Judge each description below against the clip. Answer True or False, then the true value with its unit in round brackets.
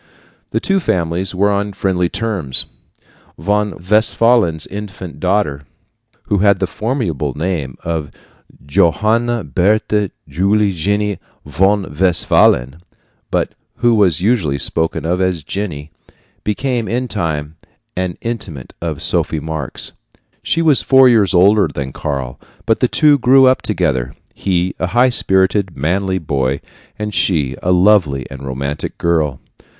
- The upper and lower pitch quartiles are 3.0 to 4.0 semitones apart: False (5.1 semitones)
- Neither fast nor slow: False (130 wpm)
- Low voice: True (95 Hz)